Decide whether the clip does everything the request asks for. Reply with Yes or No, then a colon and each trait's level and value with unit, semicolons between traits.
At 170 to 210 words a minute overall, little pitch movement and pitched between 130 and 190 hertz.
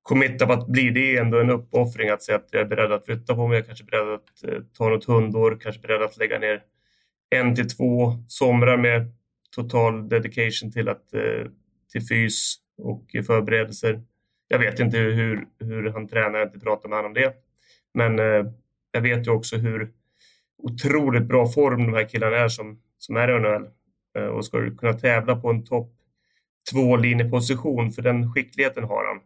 No: fast, 195 wpm; narrow, 1.9 semitones; low, 115 Hz